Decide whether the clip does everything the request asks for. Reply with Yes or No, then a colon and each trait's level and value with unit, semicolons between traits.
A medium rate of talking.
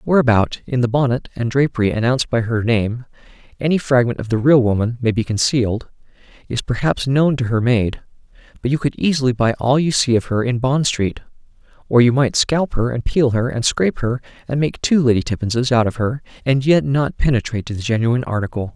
No: fast, 210 wpm